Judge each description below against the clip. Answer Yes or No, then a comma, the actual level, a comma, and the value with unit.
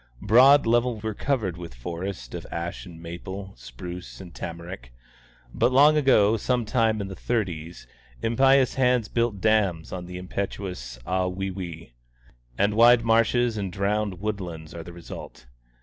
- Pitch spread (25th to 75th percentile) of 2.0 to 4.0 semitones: No, average, 4.7 semitones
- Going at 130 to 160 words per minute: Yes, average, 150 wpm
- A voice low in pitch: Yes, low, 100 Hz